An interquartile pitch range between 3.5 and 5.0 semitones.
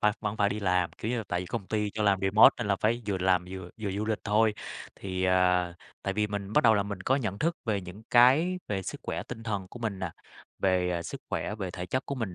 No: average, 2.9 semitones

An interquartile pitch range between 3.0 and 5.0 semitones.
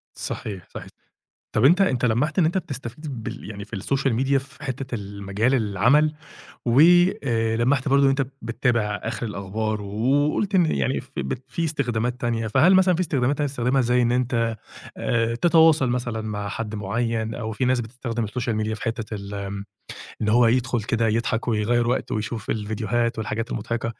Yes: average, 3.4 semitones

